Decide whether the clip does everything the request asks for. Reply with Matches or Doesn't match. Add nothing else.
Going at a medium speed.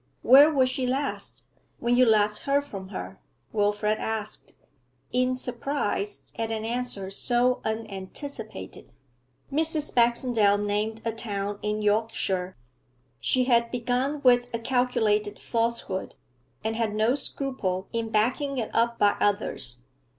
Doesn't match